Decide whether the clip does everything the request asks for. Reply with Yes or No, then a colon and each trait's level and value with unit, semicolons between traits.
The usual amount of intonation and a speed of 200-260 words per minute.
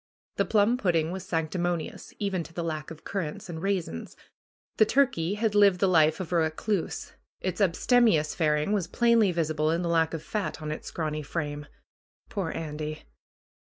No: average, 4.1 semitones; average, 170 wpm